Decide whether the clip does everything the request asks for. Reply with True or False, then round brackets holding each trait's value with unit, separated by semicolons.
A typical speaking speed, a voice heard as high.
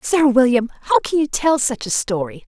False (210 wpm; 255 Hz)